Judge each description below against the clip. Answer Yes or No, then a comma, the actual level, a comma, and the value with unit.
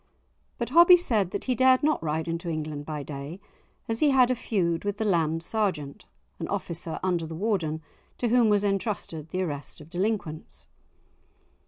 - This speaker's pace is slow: No, average, 175 wpm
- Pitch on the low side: No, medium, 185 Hz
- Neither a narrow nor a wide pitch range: No, wide, 6.0 semitones